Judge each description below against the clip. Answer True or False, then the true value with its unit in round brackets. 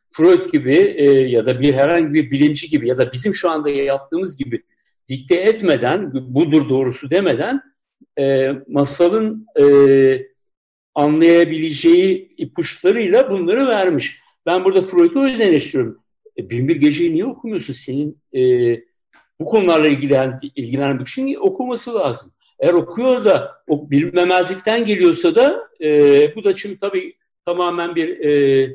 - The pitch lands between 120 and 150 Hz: False (180 Hz)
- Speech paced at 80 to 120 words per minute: False (130 wpm)